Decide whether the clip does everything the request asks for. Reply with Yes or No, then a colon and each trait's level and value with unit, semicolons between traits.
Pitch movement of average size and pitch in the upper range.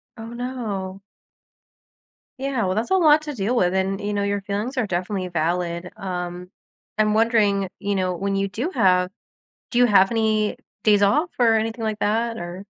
Yes: average, 3.3 semitones; high, 205 Hz